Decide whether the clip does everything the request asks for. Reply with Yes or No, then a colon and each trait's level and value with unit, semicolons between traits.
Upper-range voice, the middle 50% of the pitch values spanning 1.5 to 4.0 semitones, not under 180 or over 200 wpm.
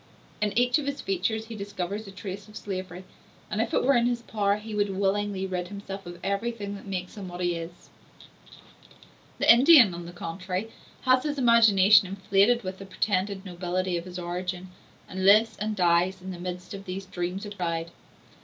Yes: high, 195 Hz; average, 2.7 semitones; average, 190 wpm